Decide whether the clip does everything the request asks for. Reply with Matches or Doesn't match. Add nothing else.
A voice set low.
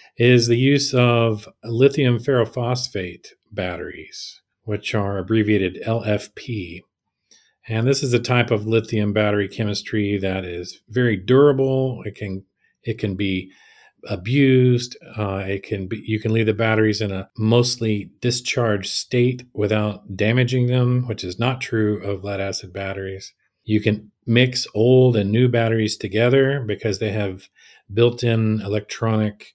Matches